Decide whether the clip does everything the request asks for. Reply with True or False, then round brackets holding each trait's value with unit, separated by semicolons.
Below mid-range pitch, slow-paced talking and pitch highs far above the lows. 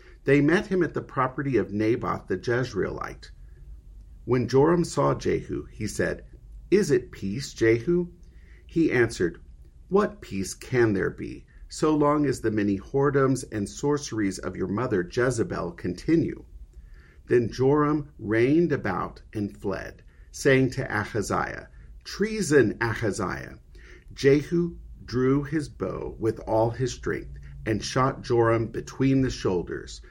True (115 Hz; 130 wpm; 7.0 semitones)